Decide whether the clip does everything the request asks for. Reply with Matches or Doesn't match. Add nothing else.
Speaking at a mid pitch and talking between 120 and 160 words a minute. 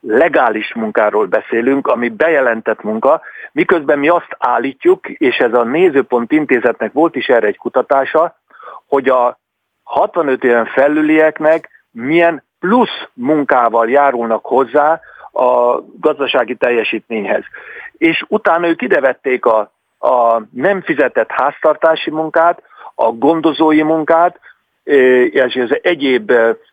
Doesn't match